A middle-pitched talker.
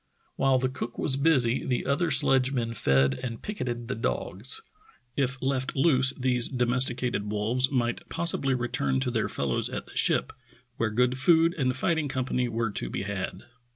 No: low, 130 Hz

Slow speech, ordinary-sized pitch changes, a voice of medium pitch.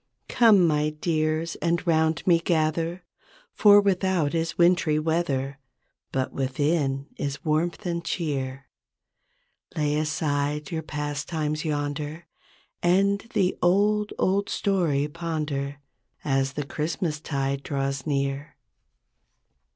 Yes: slow, 105 wpm; average, 3.1 semitones; medium, 155 Hz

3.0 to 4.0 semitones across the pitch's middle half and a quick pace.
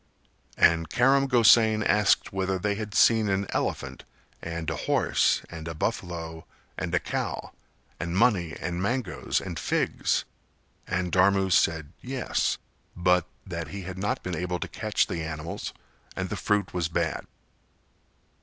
No: average, 3.7 semitones; average, 145 wpm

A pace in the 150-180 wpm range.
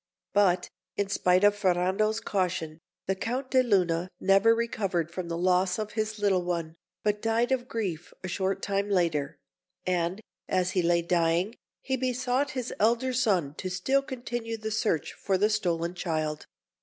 Yes: average, 165 wpm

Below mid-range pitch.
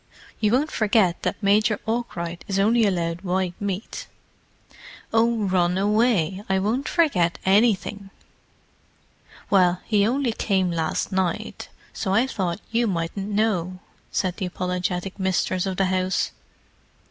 No: high, 195 Hz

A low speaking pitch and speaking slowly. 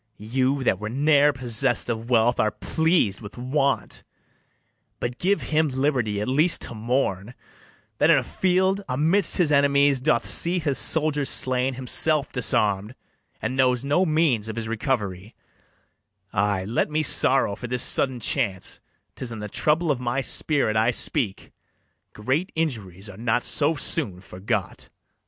No: low, 130 Hz; average, 150 wpm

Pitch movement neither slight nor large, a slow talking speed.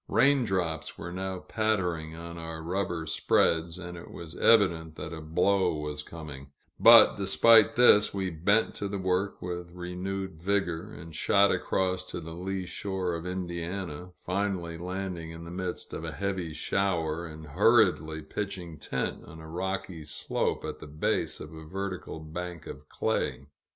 No: average, 3.0 semitones; average, 160 wpm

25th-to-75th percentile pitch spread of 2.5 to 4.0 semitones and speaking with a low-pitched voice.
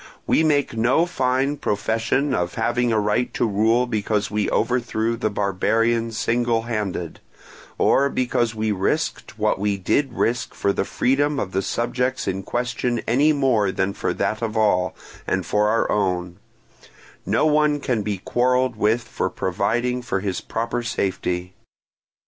Yes: average, 3.3 semitones; low, 115 Hz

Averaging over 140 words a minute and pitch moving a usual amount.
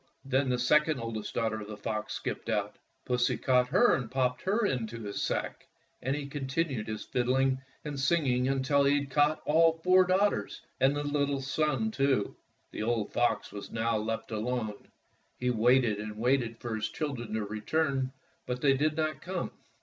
Yes: average, 180 wpm; average, 4.3 semitones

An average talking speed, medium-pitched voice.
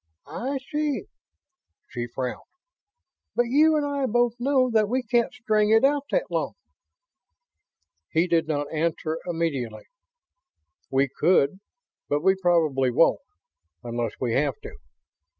No: slow, 130 wpm; medium, 180 Hz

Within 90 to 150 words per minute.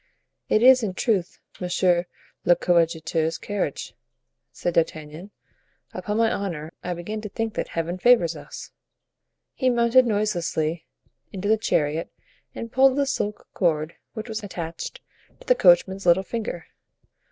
Yes: average, 140 wpm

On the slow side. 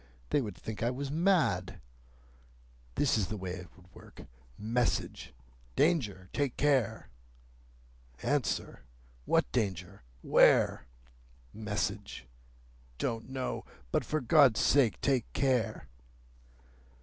Yes: slow, 100 wpm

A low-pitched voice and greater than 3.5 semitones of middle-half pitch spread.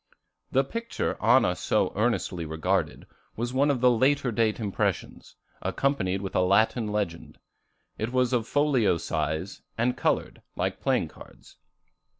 Yes: low, 115 Hz; average, 5.0 semitones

